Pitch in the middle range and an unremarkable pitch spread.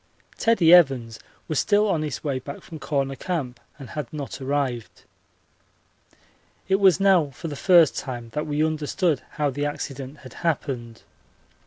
Yes: medium, 145 Hz; average, 3.9 semitones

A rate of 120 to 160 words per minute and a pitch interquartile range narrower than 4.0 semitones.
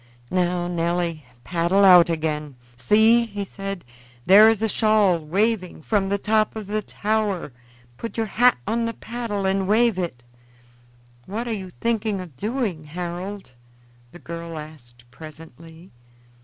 No: average, 140 wpm; average, 4.5 semitones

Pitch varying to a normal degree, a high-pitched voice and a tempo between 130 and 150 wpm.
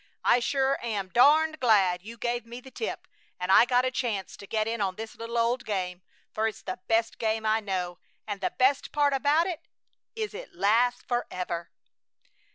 No: average, 4.2 semitones; high, 230 Hz; average, 190 wpm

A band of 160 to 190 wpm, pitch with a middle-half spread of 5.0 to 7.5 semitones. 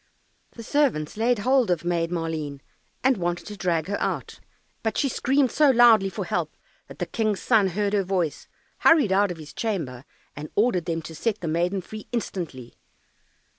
Yes: average, 180 wpm; wide, 5.4 semitones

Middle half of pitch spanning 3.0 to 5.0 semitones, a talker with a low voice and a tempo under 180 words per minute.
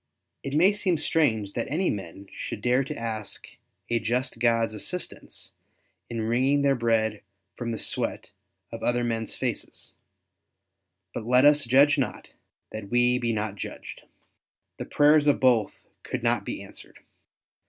Yes: average, 4.2 semitones; low, 120 Hz; average, 150 wpm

